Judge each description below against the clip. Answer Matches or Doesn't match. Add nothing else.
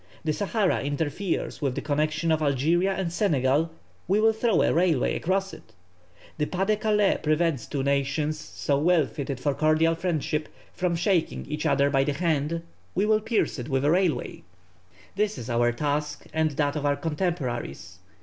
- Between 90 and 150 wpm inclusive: Doesn't match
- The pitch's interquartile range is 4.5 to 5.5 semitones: Doesn't match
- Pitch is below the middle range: Doesn't match